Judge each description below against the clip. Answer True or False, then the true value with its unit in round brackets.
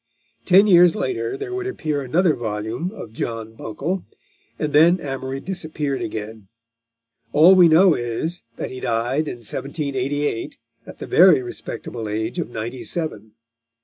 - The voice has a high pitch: False (145 Hz)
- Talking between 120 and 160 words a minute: True (145 wpm)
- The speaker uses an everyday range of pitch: False (7.0 semitones)